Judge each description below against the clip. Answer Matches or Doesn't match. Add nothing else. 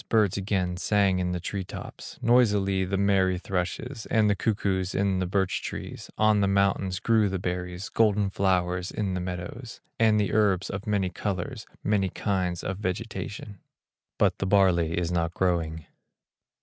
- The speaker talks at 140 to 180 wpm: Matches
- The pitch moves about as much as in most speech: Doesn't match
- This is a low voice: Matches